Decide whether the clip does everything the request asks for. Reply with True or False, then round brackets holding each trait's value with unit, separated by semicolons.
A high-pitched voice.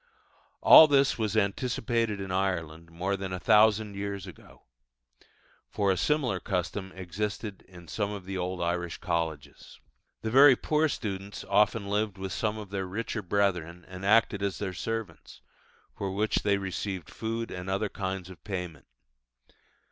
False (100 Hz)